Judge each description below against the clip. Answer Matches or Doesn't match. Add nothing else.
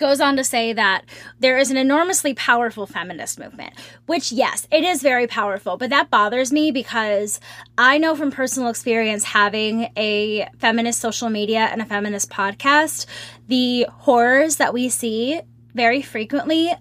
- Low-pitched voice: Doesn't match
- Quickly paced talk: Doesn't match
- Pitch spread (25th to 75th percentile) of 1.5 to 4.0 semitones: Doesn't match